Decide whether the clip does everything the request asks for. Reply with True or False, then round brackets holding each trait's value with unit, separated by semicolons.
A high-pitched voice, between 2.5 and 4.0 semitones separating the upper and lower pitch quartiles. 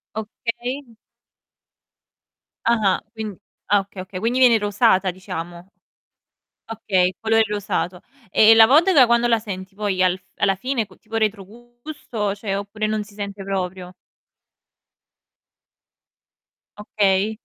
True (210 Hz; 2.8 semitones)